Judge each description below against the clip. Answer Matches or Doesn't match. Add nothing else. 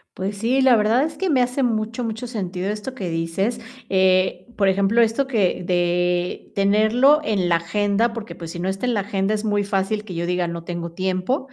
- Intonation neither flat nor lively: Matches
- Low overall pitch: Doesn't match